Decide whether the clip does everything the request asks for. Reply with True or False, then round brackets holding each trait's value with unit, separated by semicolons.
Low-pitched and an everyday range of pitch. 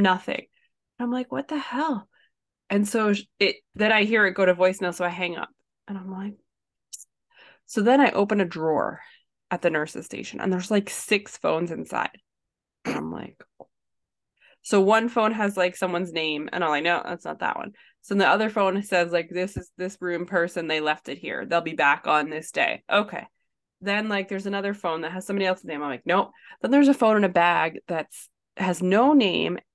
False (190 Hz; 3.4 semitones)